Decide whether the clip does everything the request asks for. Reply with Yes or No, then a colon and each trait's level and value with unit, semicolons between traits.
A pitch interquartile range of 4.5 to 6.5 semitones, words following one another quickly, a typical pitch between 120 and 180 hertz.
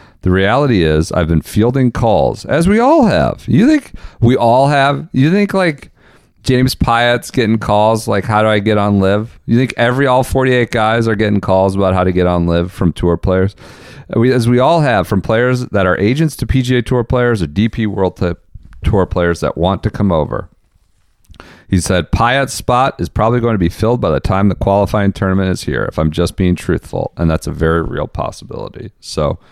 No: wide, 5.5 semitones; fast, 210 wpm; low, 105 Hz